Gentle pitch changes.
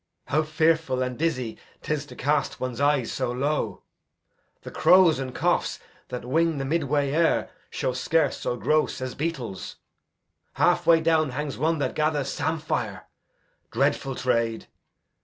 No: average, 3.8 semitones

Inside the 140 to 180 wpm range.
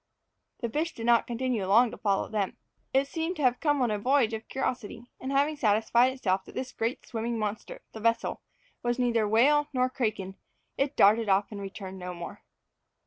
No: average, 195 wpm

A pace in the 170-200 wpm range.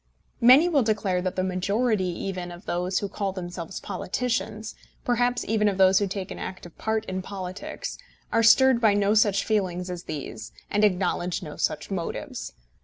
Yes: average, 175 wpm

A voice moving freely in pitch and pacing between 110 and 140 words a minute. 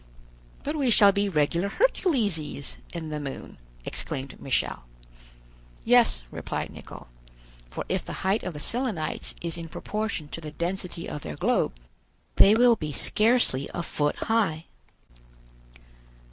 Yes: wide, 6.3 semitones; slow, 135 wpm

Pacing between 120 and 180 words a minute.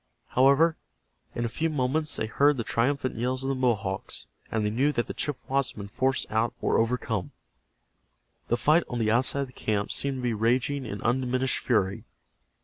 No: average, 190 wpm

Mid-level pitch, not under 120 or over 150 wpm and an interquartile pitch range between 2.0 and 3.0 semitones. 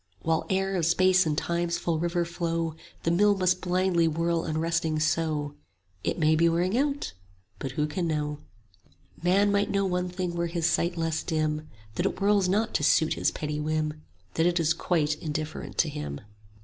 No: medium, 170 Hz; average, 190 wpm; average, 2.7 semitones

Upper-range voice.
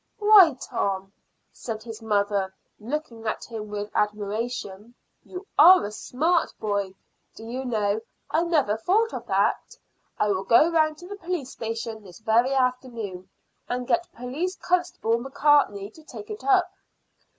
Yes: high, 235 Hz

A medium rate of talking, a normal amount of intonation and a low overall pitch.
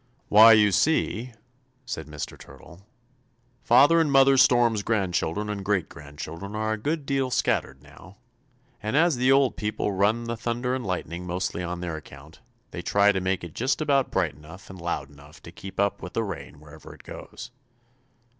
No: average, 180 wpm; wide, 5.7 semitones; low, 100 Hz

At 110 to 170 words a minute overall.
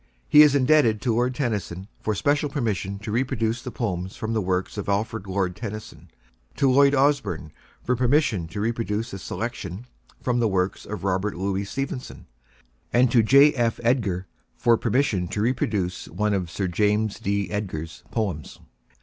Yes: average, 165 wpm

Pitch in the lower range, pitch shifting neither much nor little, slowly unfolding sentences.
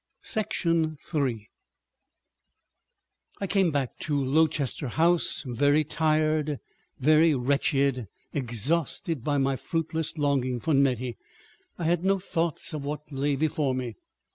No: medium, 145 Hz; average, 3.1 semitones; slow, 115 wpm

